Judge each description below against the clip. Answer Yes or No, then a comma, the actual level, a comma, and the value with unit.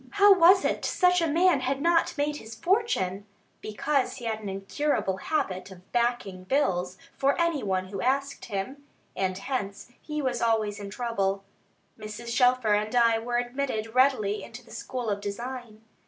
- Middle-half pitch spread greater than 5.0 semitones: Yes, wide, 5.4 semitones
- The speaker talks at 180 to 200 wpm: No, average, 170 wpm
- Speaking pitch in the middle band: No, high, 235 Hz